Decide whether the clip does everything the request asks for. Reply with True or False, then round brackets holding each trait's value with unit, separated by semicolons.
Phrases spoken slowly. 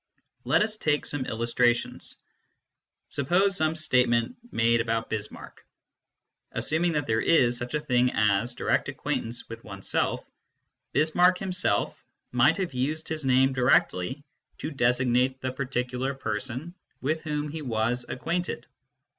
True (130 wpm)